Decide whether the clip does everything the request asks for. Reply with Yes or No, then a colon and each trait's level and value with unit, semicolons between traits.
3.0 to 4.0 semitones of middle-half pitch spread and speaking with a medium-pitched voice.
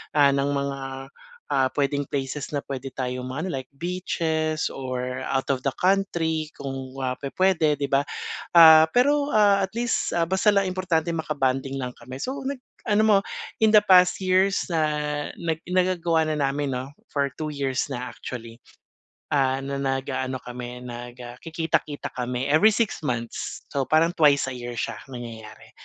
No: average, 4.5 semitones; medium, 145 Hz